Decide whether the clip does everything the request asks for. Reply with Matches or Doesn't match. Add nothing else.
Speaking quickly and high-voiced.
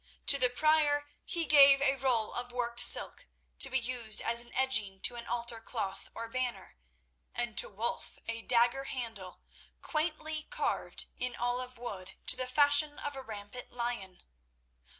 Doesn't match